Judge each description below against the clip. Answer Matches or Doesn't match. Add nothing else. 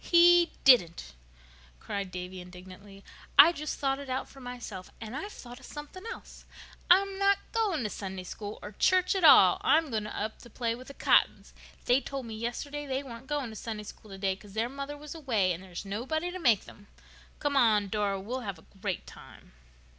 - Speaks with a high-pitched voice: Matches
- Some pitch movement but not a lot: Doesn't match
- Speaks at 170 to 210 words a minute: Matches